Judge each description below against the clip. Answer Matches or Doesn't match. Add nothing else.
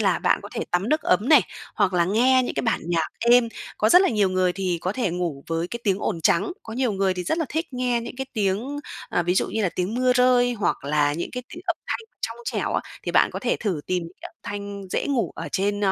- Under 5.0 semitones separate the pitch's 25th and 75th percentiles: Doesn't match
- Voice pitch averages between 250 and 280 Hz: Doesn't match